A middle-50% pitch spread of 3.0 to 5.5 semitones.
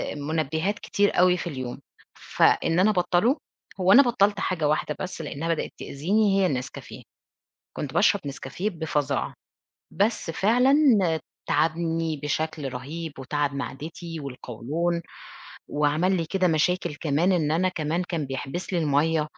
Yes: average, 3.7 semitones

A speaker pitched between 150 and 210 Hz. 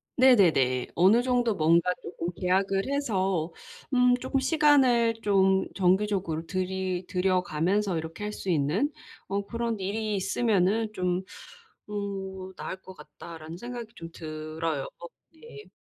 Yes: high, 190 Hz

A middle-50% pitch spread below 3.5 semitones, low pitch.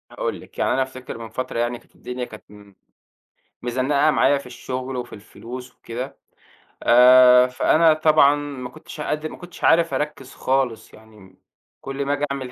Yes: average, 2.8 semitones; low, 130 Hz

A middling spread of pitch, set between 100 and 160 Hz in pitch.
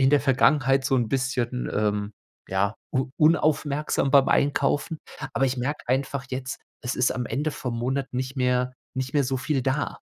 No: narrow, 1.8 semitones; low, 130 Hz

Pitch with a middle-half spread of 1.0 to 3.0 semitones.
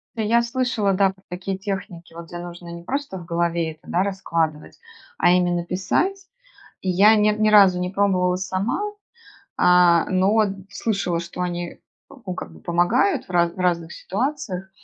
Yes: average, 2.7 semitones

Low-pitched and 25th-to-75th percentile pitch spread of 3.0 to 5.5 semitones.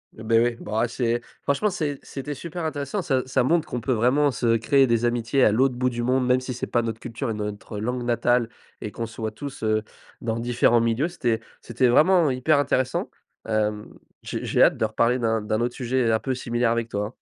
No: low, 120 Hz; narrow, 2.6 semitones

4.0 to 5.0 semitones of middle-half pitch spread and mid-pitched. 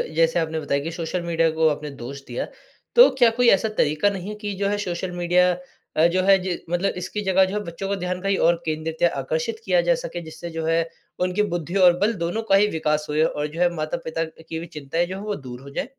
No: average, 3.5 semitones; medium, 175 Hz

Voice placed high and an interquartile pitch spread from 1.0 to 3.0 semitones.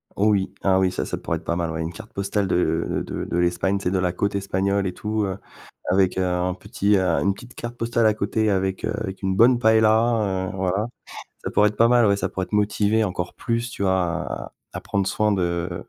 No: low, 100 Hz; average, 2.7 semitones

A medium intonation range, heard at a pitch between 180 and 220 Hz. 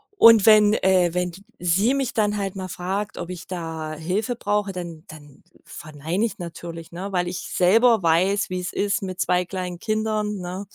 Yes: average, 3.1 semitones; medium, 185 Hz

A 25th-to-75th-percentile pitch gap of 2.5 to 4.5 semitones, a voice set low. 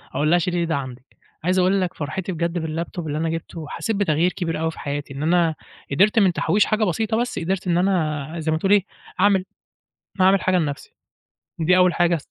No: average, 3.2 semitones; medium, 170 Hz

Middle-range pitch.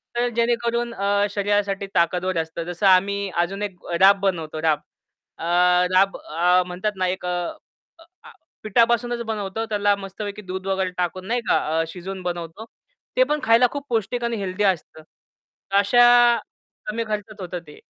No: high, 200 Hz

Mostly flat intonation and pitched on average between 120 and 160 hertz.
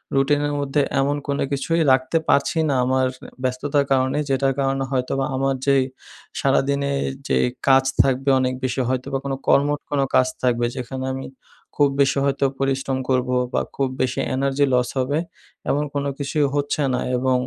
Yes: narrow, 1.3 semitones; low, 135 Hz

